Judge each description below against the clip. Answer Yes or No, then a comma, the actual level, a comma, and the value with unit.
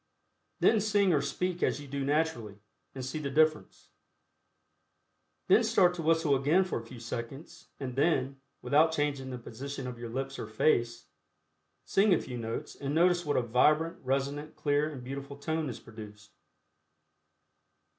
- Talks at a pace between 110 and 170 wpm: Yes, average, 160 wpm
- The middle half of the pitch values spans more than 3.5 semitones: Yes, average, 4.2 semitones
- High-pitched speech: No, medium, 140 Hz